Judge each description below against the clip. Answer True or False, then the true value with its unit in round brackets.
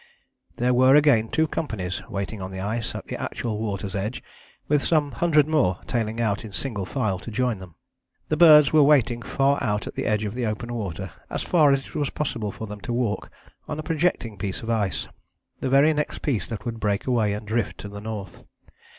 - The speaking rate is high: True (215 wpm)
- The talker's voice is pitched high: False (115 Hz)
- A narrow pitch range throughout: False (5.2 semitones)